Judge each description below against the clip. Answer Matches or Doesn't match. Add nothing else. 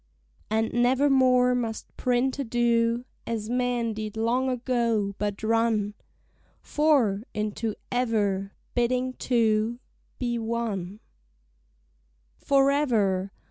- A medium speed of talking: Doesn't match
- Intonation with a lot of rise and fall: Doesn't match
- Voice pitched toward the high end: Matches